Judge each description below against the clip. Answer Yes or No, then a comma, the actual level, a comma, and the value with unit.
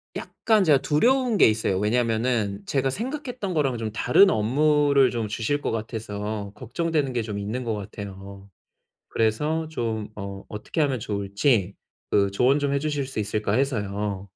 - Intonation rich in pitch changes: Yes, wide, 5.8 semitones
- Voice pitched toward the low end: Yes, low, 115 Hz